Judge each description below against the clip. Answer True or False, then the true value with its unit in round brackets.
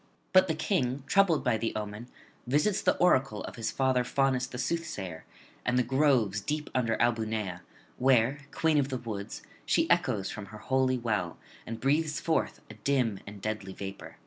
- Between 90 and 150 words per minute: False (170 wpm)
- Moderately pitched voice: False (125 Hz)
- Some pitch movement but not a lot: True (4.5 semitones)